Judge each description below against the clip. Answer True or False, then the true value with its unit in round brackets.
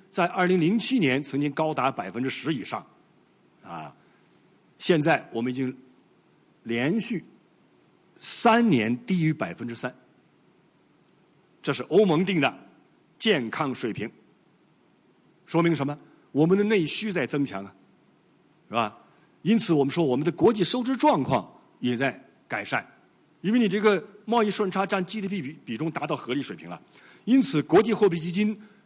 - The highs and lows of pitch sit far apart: True (7.1 semitones)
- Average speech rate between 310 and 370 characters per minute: False (220 characters per minute)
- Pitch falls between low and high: True (175 Hz)